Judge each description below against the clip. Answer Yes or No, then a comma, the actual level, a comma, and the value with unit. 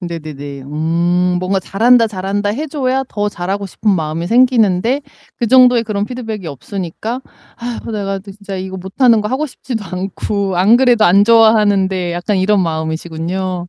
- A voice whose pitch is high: Yes, high, 195 Hz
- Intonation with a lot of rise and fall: No, average, 4.2 semitones